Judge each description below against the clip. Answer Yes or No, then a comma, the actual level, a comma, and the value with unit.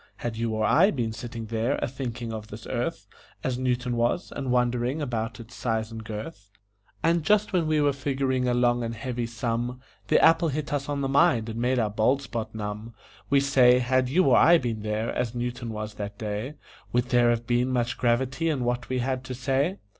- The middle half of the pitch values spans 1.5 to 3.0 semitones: Yes, average, 2.7 semitones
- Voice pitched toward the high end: No, low, 125 Hz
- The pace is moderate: No, fast, 215 wpm